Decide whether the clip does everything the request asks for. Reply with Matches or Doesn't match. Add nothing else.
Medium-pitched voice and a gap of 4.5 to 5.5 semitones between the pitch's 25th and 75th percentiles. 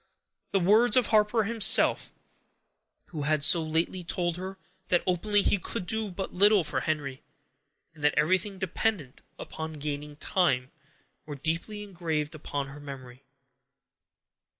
Matches